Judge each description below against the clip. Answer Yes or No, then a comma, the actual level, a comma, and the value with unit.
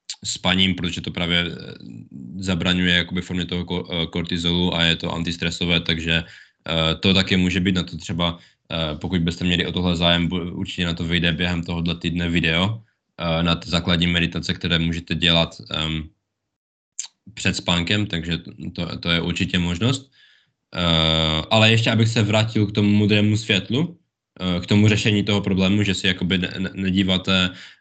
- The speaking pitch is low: Yes, very low, 90 Hz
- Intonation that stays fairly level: Yes, narrow, 2.1 semitones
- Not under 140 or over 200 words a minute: Yes, average, 145 wpm